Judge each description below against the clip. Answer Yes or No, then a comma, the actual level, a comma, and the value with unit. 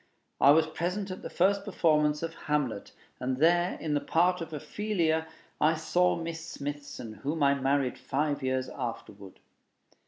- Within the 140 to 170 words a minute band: Yes, average, 155 wpm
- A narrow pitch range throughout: No, average, 3.2 semitones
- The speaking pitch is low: No, medium, 155 Hz